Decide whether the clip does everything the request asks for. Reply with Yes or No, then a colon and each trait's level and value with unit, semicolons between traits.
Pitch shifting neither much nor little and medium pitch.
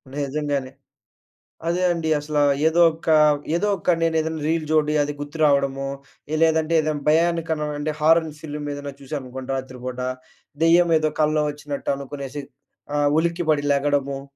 No: narrow, 2.3 semitones; medium, 150 Hz